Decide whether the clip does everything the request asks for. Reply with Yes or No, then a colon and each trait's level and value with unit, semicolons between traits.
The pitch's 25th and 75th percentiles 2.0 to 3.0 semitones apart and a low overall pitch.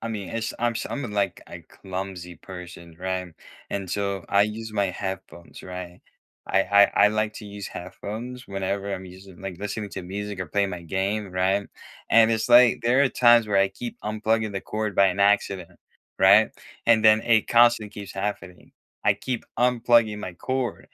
Yes: average, 2.7 semitones; low, 100 Hz